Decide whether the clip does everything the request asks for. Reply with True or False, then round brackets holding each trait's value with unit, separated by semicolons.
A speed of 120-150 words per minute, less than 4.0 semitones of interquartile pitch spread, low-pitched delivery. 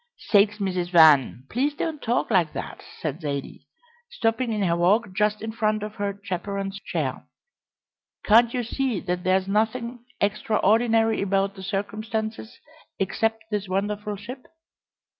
False (140 wpm; 2.7 semitones; 210 Hz)